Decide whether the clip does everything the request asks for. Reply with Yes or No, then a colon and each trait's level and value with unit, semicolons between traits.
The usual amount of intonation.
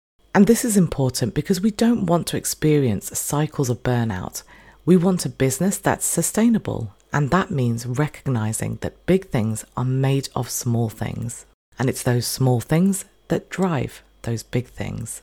No: wide, 6.8 semitones